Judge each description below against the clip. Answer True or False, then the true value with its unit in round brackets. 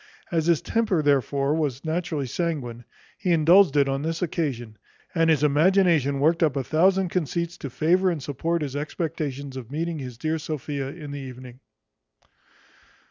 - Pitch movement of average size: True (3.5 semitones)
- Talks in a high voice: False (150 Hz)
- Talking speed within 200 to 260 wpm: False (160 wpm)